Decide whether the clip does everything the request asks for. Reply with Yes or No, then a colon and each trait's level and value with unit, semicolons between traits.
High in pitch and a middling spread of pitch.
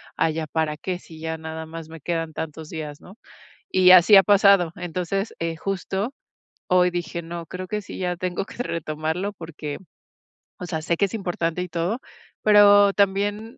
No: medium, 175 Hz; average, 3.4 semitones